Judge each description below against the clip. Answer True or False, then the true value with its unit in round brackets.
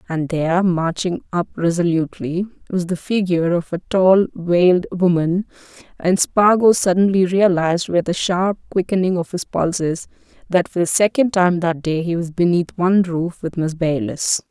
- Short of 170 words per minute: True (160 wpm)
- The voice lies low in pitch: False (175 Hz)